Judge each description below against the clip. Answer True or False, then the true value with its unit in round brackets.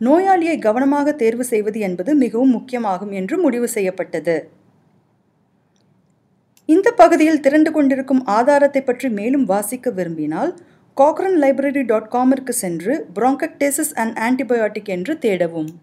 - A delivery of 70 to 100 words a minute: False (110 wpm)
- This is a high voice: True (255 Hz)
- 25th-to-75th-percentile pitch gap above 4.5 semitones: True (5.4 semitones)